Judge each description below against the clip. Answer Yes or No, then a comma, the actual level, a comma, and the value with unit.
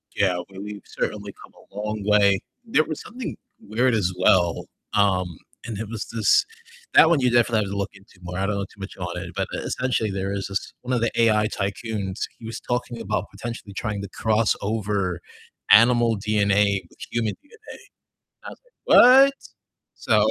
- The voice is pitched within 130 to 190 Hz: No, low, 105 Hz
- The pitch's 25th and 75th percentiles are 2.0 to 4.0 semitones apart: Yes, average, 2.9 semitones